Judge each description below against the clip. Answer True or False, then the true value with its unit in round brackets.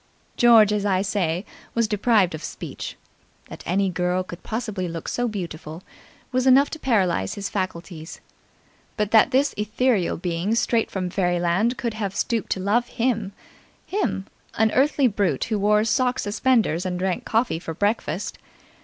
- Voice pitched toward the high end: True (205 Hz)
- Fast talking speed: False (155 wpm)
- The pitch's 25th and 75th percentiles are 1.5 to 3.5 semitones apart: False (4.3 semitones)